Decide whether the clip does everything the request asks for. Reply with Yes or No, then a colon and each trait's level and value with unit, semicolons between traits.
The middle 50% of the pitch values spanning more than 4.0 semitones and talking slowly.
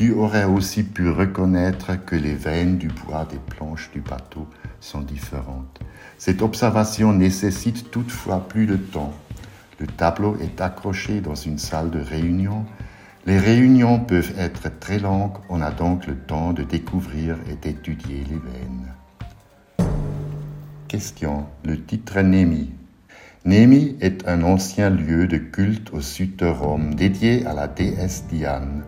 Yes: average, 4.7 semitones; slow, 140 wpm